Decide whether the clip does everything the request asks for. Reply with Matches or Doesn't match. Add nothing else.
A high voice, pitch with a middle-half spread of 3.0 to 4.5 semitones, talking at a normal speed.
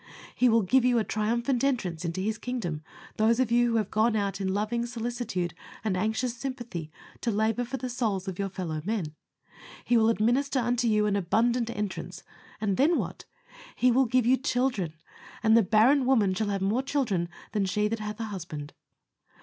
Matches